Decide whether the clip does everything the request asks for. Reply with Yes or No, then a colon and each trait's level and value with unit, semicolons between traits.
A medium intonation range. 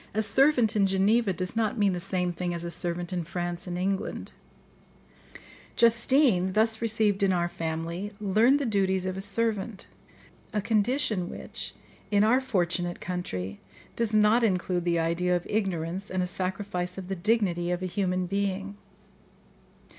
Yes: average, 3.3 semitones